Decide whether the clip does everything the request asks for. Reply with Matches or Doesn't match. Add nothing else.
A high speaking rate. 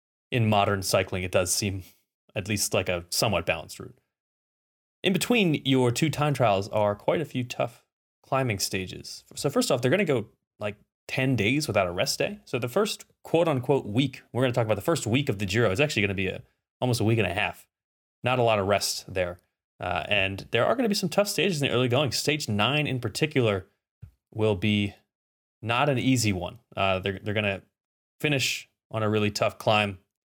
Matches